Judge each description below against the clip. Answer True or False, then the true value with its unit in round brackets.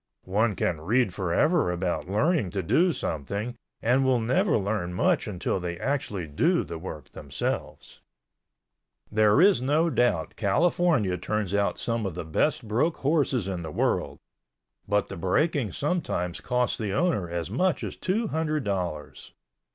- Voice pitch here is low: True (105 Hz)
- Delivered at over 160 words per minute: False (150 wpm)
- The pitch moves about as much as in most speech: False (8.4 semitones)